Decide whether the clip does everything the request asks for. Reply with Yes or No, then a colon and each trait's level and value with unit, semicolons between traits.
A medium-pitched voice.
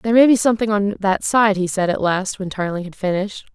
No: high, 200 Hz